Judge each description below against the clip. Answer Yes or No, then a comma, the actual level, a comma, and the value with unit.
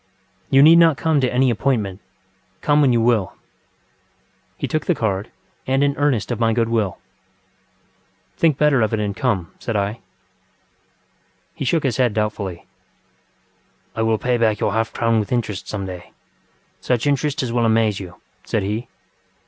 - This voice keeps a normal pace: Yes, average, 165 wpm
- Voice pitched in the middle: No, low, 115 Hz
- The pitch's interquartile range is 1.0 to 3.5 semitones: No, average, 4.2 semitones